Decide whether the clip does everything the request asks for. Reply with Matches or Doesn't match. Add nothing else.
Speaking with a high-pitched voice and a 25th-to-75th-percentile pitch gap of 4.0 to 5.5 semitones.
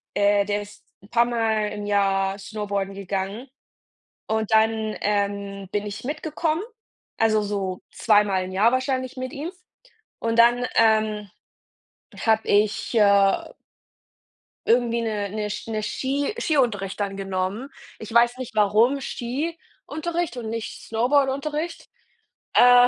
Doesn't match